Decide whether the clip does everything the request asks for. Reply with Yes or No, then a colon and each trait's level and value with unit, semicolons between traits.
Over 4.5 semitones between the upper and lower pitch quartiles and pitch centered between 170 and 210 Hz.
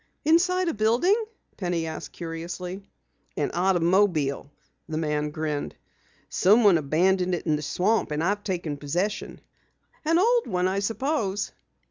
Yes: average, 5.1 semitones; medium, 185 Hz